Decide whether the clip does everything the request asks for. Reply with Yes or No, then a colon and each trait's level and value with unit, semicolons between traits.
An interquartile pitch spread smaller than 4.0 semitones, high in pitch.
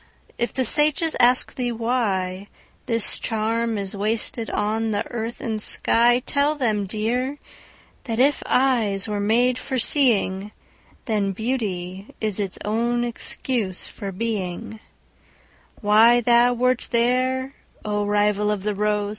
Yes: average, 2.9 semitones; high, 225 Hz